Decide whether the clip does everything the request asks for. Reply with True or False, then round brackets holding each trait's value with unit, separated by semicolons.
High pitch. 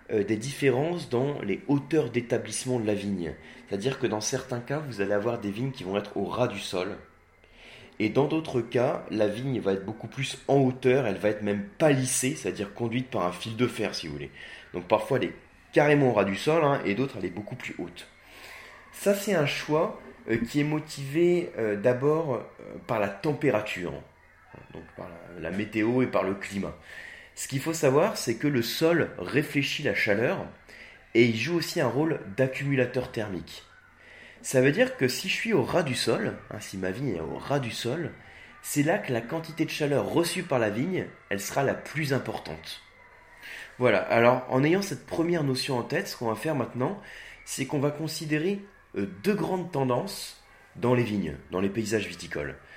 False (125 Hz)